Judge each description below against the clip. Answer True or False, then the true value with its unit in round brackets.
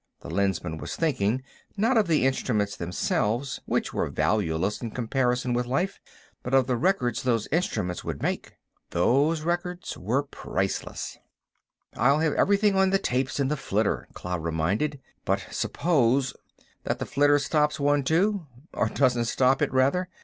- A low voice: True (130 Hz)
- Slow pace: False (150 wpm)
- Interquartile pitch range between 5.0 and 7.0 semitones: True (5.6 semitones)